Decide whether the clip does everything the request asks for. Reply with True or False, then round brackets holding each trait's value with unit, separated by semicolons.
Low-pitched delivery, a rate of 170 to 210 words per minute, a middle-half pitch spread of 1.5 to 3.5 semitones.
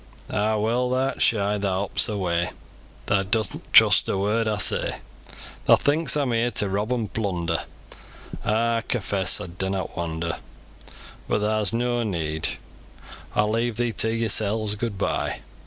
False (105 Hz; 150 wpm; 3.1 semitones)